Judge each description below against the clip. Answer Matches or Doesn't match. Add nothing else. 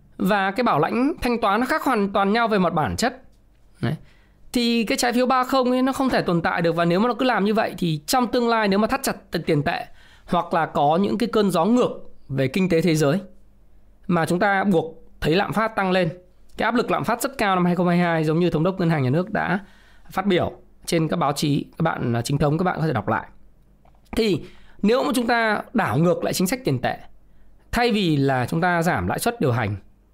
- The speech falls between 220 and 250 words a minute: Matches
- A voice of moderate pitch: Matches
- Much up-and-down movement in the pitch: Matches